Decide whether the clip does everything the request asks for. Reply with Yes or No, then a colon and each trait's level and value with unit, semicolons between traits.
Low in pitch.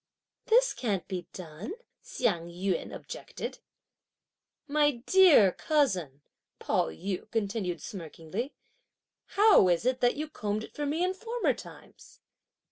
No: high, 220 Hz